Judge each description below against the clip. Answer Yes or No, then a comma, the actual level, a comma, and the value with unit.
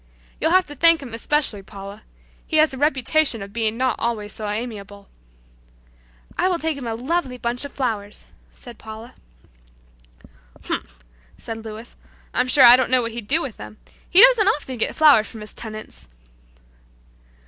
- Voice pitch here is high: Yes, high, 240 Hz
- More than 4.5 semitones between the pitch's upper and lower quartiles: Yes, average, 5.3 semitones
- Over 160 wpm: Yes, average, 170 wpm